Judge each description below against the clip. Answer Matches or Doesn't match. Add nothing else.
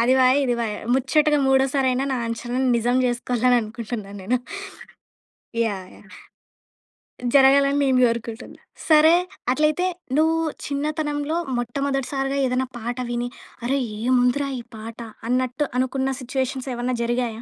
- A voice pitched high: Matches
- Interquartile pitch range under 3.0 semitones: Matches